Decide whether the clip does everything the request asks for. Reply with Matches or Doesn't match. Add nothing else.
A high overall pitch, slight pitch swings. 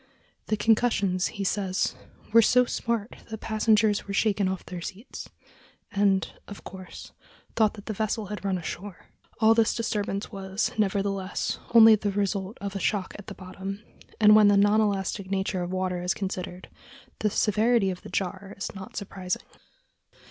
Matches